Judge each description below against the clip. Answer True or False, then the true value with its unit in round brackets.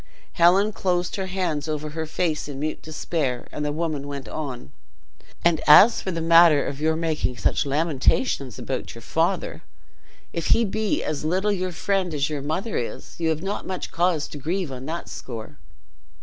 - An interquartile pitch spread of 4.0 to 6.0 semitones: False (3.6 semitones)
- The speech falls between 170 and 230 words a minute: True (180 wpm)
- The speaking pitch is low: False (160 Hz)